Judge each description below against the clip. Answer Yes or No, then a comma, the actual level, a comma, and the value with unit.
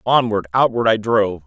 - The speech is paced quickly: No, average, 165 wpm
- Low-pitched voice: Yes, low, 110 Hz